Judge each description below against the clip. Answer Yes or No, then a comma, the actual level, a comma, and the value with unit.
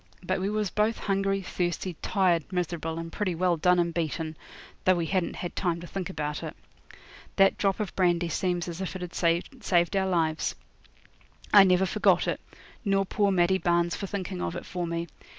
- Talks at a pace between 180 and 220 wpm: Yes, average, 190 wpm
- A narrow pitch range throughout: Yes, narrow, 2.2 semitones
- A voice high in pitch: No, medium, 180 Hz